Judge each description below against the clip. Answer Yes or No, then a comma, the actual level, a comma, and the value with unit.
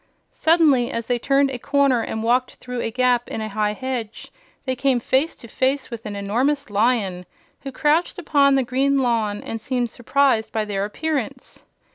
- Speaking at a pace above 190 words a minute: No, average, 180 wpm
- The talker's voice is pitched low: No, very high, 250 Hz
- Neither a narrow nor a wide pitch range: Yes, average, 3.7 semitones